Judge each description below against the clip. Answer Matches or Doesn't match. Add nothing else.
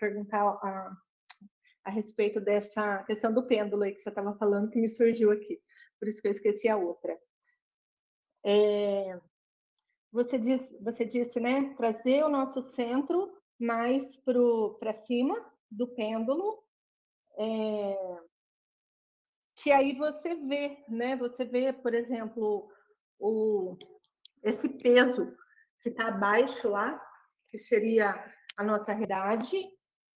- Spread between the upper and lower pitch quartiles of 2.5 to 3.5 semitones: Doesn't match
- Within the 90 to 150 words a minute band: Matches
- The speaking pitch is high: Matches